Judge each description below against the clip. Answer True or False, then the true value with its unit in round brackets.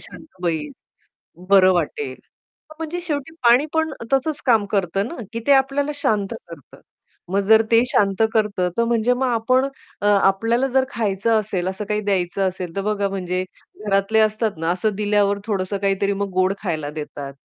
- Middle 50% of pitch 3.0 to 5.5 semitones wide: True (3.5 semitones)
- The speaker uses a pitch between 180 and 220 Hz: True (205 Hz)